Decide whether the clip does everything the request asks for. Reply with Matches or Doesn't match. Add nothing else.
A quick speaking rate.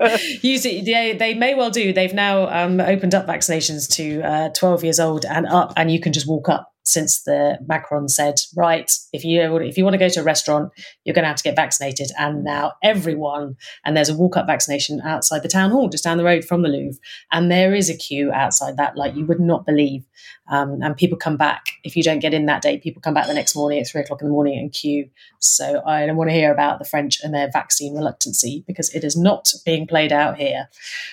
Matches